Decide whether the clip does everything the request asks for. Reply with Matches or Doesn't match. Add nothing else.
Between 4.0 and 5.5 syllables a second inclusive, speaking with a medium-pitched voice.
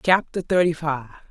Matches